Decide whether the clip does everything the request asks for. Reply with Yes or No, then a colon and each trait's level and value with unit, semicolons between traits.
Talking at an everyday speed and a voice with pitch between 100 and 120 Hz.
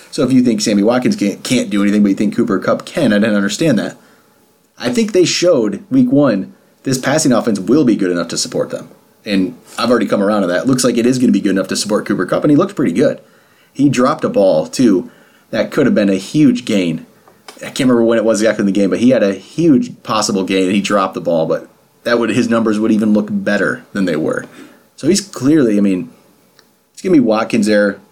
No: fast, 250 wpm; low, 115 Hz